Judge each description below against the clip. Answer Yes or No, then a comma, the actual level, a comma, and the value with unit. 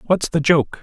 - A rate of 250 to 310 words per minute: No, fast, 215 wpm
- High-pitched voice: No, medium, 155 Hz